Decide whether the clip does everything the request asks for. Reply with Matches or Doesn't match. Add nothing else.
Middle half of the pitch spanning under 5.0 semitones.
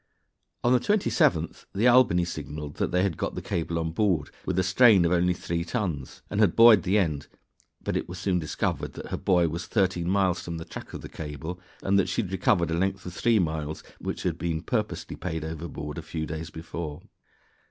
Matches